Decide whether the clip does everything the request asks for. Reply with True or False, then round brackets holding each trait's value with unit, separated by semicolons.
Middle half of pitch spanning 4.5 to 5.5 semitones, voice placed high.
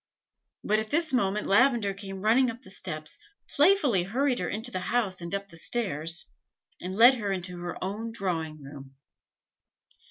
True (5.0 semitones; 200 Hz)